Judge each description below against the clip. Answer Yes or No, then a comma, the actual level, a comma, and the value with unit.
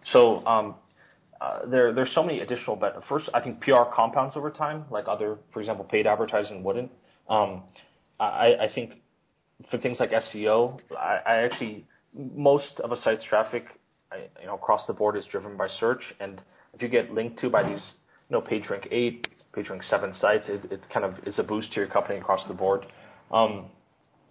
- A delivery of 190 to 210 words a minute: Yes, average, 195 wpm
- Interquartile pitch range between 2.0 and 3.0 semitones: No, average, 4.8 semitones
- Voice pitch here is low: Yes, low, 120 Hz